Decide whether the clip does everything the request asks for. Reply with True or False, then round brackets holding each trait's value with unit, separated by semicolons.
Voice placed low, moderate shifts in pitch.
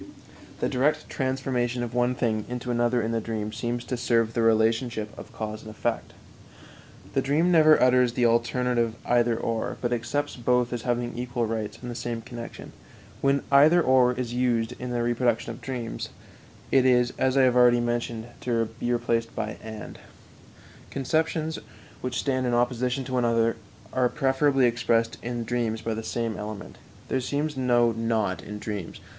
False (120 Hz; 1.8 semitones)